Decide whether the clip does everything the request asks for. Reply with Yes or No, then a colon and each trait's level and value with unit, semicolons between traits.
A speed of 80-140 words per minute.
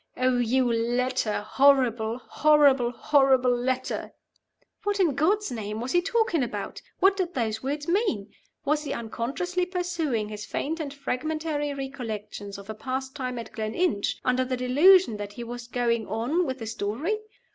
No: average, 155 wpm